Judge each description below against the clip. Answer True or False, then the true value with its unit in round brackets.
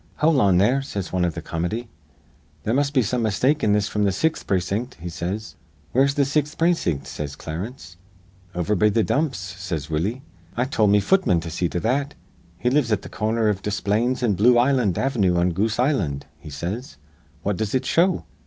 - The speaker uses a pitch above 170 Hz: False (105 Hz)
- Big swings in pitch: True (6.1 semitones)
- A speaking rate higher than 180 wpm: True (200 wpm)